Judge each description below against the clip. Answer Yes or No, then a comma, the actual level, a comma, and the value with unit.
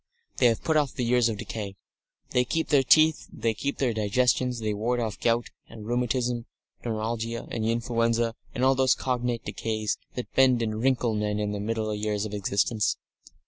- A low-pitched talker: Yes, low, 115 Hz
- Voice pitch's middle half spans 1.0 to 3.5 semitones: Yes, narrow, 2.4 semitones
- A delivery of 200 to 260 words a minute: No, average, 190 wpm